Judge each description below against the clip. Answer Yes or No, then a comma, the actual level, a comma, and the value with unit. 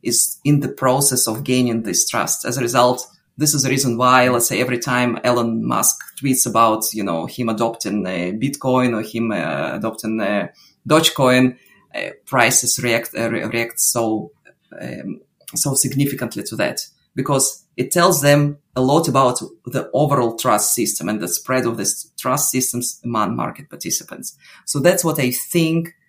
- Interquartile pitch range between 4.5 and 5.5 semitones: No, average, 3.3 semitones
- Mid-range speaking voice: No, low, 125 Hz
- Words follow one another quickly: No, average, 170 wpm